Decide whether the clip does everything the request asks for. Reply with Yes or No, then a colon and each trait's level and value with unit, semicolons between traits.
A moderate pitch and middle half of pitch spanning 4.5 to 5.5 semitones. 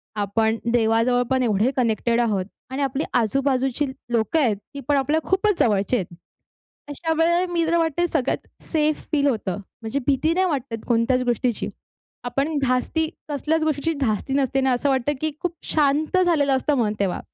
No: very high, 270 Hz; average, 4.9 semitones